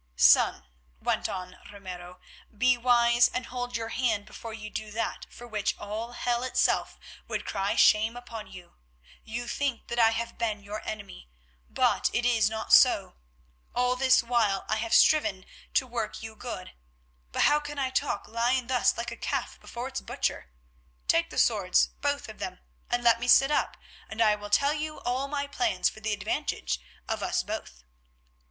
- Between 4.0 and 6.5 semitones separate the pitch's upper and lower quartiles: No, average, 2.8 semitones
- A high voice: Yes, high, 235 Hz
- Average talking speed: Yes, average, 180 wpm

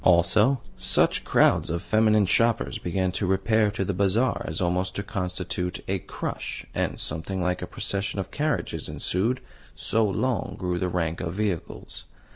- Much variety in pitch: No, average, 3.1 semitones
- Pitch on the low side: Yes, very low, 95 Hz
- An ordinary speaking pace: Yes, average, 160 wpm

